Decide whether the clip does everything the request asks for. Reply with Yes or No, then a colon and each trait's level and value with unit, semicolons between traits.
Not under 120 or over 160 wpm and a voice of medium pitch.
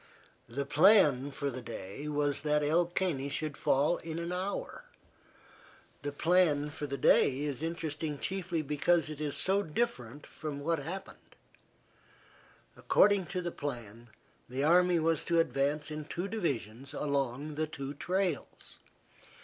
Yes: average, 140 wpm; medium, 150 Hz